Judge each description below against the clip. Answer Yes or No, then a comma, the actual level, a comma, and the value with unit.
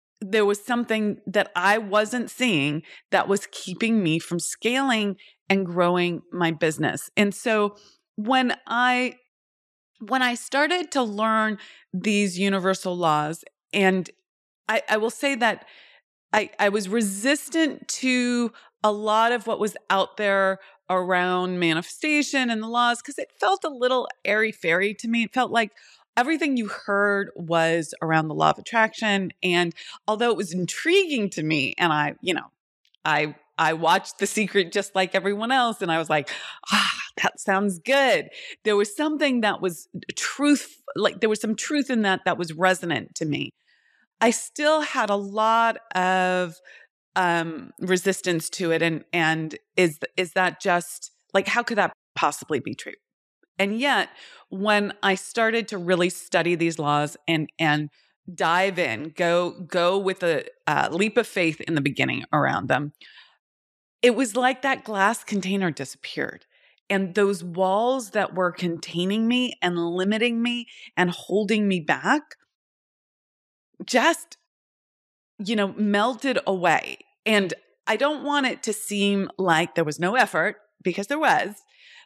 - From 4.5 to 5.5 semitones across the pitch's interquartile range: Yes, average, 4.9 semitones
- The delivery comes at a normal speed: Yes, average, 155 wpm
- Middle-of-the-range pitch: No, high, 200 Hz